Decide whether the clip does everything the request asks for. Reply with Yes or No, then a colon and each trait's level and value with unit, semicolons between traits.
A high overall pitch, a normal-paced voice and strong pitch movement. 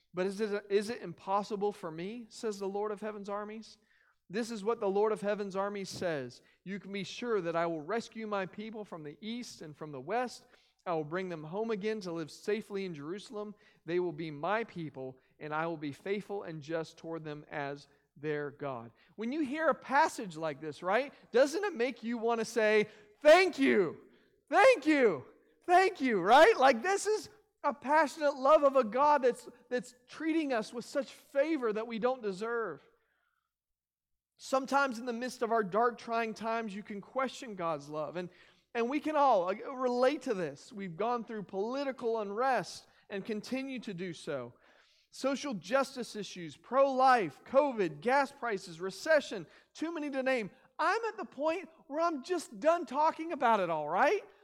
Yes: high, 220 Hz; average, 185 wpm; wide, 6.2 semitones